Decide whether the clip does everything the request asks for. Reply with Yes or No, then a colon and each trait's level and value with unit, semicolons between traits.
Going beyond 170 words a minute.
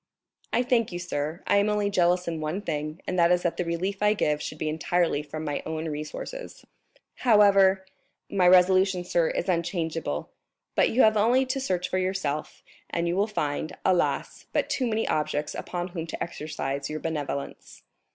Yes: average, 180 wpm